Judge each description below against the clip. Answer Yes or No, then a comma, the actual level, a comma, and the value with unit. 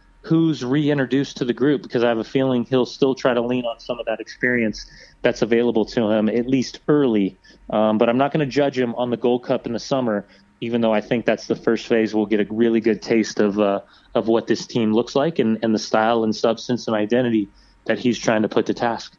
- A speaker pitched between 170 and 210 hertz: No, low, 115 Hz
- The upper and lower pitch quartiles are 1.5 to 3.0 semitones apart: Yes, narrow, 2.4 semitones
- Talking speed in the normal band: No, fast, 245 wpm